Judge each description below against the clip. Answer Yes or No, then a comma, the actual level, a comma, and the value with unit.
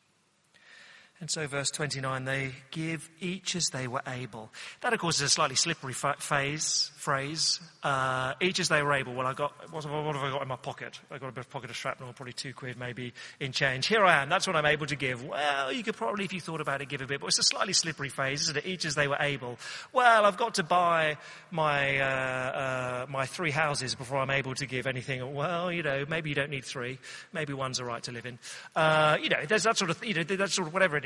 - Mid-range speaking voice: Yes, medium, 145 Hz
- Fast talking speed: Yes, fast, 255 wpm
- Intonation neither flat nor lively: Yes, average, 3.5 semitones